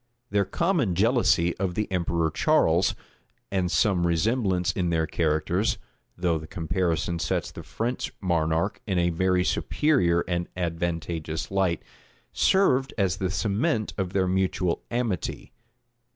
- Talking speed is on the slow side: Yes, slow, 130 wpm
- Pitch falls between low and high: No, very low, 90 Hz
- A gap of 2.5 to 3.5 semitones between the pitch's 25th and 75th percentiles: Yes, average, 2.9 semitones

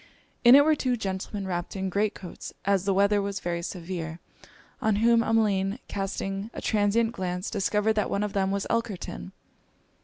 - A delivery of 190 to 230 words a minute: No, average, 175 wpm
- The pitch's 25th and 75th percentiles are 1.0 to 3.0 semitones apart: Yes, narrow, 2.5 semitones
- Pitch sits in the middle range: No, high, 200 Hz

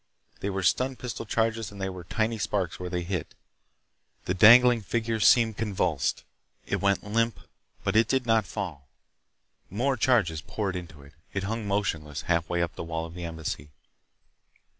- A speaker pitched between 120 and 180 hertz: No, low, 100 Hz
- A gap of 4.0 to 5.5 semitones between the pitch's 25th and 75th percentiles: Yes, average, 4.7 semitones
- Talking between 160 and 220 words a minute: Yes, average, 165 wpm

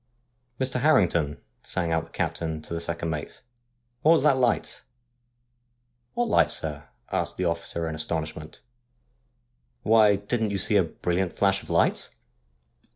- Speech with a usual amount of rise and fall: No, wide, 6.6 semitones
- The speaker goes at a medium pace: Yes, average, 170 wpm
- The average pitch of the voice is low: Yes, low, 100 Hz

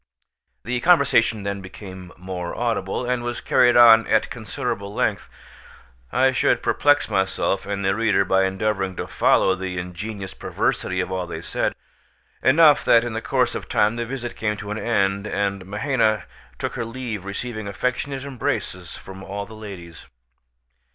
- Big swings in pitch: No, average, 3.7 semitones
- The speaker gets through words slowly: No, average, 160 wpm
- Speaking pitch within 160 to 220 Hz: No, low, 105 Hz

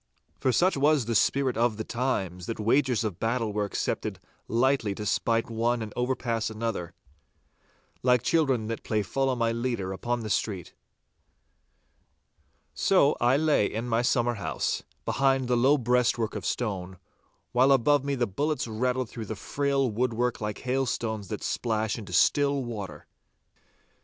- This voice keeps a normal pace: Yes, average, 150 wpm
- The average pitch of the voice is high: No, low, 120 Hz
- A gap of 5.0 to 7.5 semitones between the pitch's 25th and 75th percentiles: No, average, 3.1 semitones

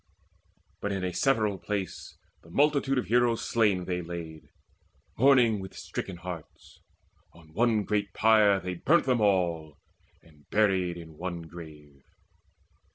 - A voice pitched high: No, very low, 95 Hz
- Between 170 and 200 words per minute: No, slow, 135 wpm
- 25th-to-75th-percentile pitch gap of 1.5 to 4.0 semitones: No, average, 4.6 semitones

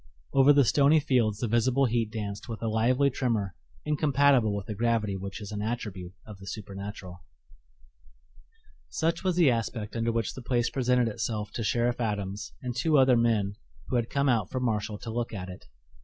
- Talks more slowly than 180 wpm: No, average, 185 wpm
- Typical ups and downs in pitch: Yes, average, 3.5 semitones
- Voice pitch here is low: Yes, low, 115 Hz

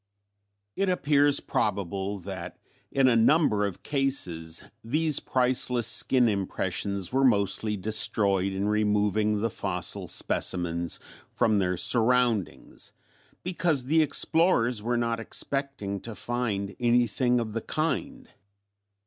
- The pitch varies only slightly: No, average, 4.8 semitones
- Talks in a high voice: No, low, 115 Hz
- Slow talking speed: Yes, slow, 115 wpm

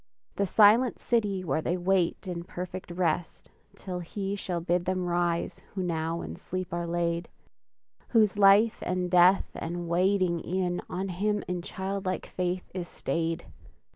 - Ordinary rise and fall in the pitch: No, narrow, 1.9 semitones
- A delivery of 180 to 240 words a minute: No, average, 150 wpm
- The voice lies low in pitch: No, medium, 180 Hz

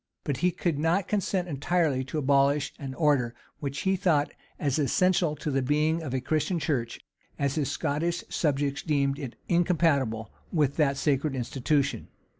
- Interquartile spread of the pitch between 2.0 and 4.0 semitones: Yes, average, 3.2 semitones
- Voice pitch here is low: No, medium, 145 Hz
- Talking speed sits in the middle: Yes, average, 160 wpm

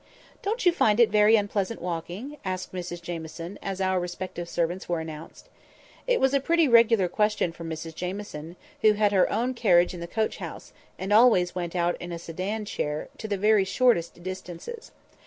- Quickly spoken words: No, average, 185 wpm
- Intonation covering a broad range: No, average, 4.0 semitones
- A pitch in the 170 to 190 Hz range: Yes, medium, 185 Hz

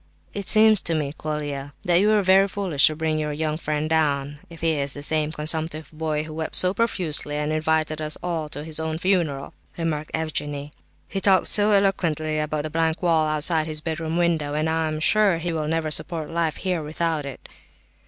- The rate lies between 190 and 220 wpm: Yes, fast, 205 wpm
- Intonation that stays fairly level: Yes, narrow, 1.9 semitones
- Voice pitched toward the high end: No, medium, 155 Hz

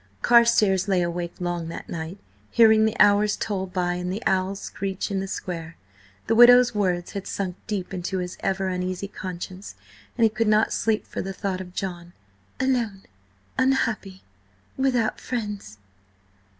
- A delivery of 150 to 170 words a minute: Yes, average, 155 wpm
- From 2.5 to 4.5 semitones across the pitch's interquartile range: Yes, average, 3.2 semitones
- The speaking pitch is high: Yes, high, 195 Hz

